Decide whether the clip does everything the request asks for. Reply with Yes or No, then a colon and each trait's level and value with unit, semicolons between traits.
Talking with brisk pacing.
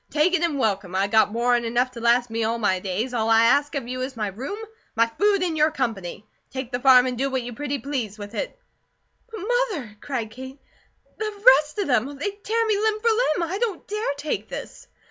Yes: fast, 230 wpm